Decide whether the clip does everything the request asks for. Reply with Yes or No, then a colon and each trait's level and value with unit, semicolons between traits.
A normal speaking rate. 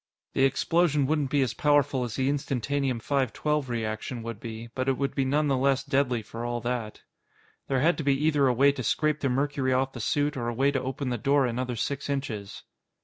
No: fast, 220 wpm